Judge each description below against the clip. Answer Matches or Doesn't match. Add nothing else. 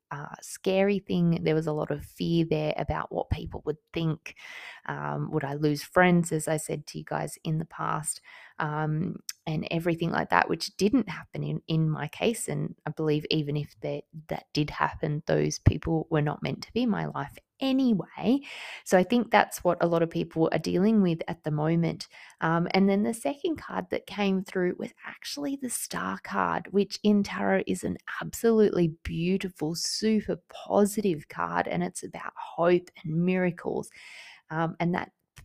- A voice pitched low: Doesn't match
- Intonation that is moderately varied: Matches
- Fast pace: Doesn't match